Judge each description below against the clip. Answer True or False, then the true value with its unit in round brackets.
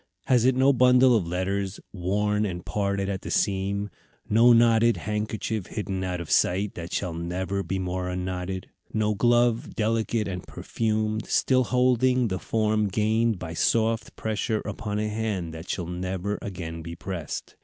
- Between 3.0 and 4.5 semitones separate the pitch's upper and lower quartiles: True (3.4 semitones)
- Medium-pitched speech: False (105 Hz)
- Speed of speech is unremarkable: True (160 wpm)